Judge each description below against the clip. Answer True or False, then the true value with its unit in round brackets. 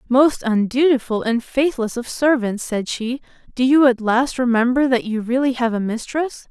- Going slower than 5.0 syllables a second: True (4.7 syllables/s)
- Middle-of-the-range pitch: False (245 Hz)